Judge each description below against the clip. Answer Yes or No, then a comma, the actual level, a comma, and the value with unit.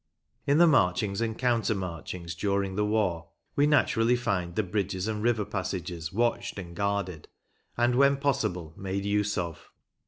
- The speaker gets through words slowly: No, average, 155 wpm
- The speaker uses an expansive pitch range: No, average, 4.5 semitones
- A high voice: No, low, 100 Hz